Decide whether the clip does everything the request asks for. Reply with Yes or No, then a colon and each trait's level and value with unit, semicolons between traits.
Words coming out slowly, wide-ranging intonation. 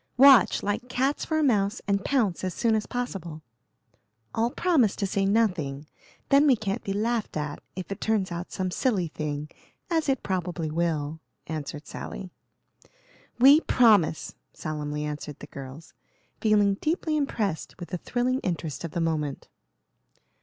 No: average, 155 wpm; wide, 7.1 semitones